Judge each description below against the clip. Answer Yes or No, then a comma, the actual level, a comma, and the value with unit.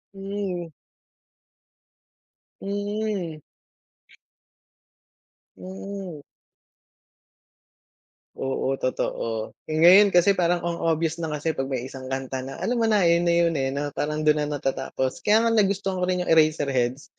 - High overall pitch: No, medium, 165 Hz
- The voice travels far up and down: Yes, wide, 5.9 semitones